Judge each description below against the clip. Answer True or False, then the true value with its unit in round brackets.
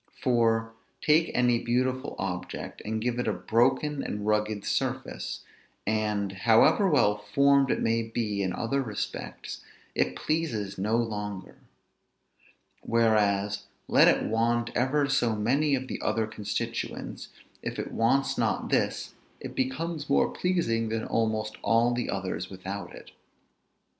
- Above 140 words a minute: False (135 wpm)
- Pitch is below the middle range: True (115 Hz)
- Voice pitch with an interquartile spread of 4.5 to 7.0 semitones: False (3.7 semitones)